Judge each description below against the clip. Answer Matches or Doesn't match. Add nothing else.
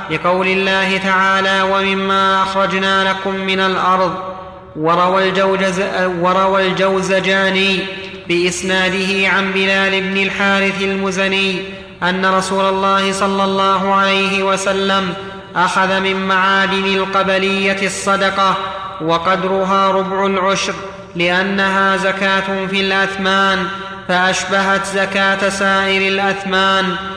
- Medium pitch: Doesn't match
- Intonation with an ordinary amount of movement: Doesn't match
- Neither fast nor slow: Matches